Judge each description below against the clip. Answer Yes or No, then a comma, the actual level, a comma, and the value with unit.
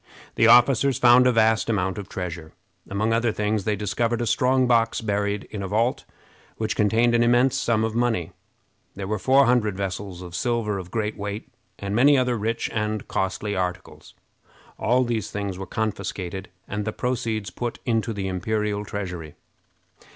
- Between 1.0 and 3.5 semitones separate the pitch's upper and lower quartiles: Yes, average, 3.0 semitones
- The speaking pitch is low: Yes, low, 110 Hz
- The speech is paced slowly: No, average, 170 wpm